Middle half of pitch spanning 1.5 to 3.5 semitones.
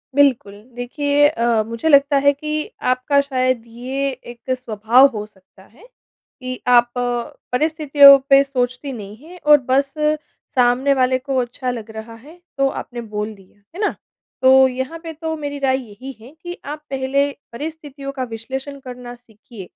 Yes: average, 2.9 semitones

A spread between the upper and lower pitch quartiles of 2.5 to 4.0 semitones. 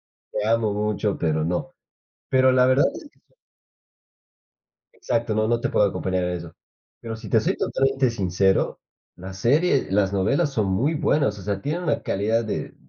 No: average, 5.2 semitones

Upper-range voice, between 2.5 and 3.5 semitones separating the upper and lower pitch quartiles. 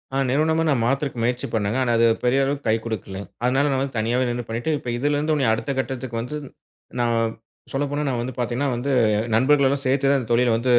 No: low, 125 Hz; average, 3.0 semitones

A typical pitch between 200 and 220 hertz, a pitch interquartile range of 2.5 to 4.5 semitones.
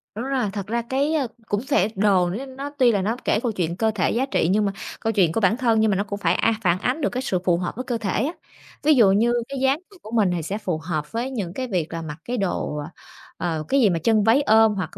No: high, 215 Hz; average, 5.0 semitones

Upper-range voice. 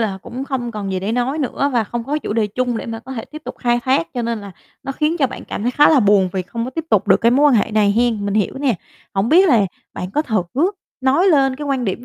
Yes: high, 240 Hz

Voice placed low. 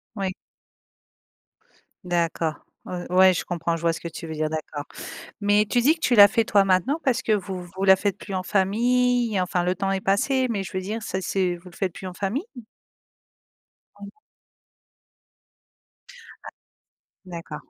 No: high, 190 Hz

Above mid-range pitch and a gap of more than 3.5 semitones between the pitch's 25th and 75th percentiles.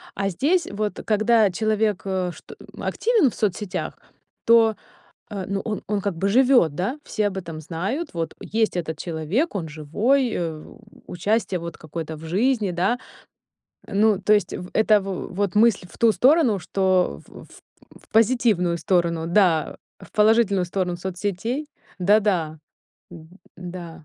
Yes: high, 195 Hz; average, 4.1 semitones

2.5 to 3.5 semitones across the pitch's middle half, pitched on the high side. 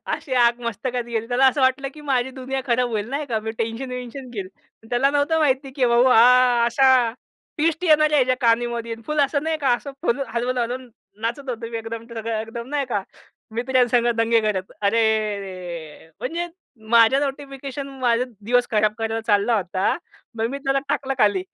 Yes: average, 3.0 semitones; high, 245 Hz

